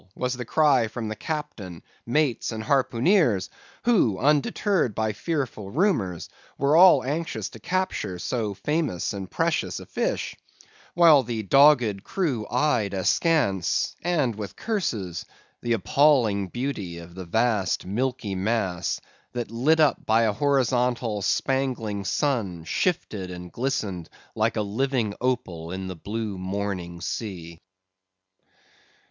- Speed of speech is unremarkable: No, slow, 125 wpm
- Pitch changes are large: Yes, wide, 6.3 semitones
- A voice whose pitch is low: Yes, low, 115 Hz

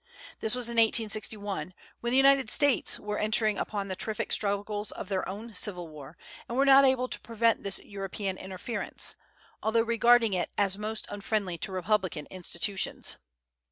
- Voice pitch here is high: Yes, high, 210 Hz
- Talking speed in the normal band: Yes, average, 160 wpm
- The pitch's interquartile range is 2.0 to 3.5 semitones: Yes, average, 3.2 semitones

